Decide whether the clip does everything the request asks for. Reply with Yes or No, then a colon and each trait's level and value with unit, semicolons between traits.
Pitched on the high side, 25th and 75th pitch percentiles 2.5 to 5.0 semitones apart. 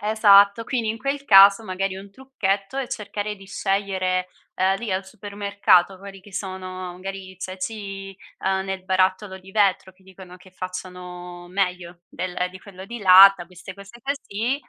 No: high, 195 Hz; narrow, 1.6 semitones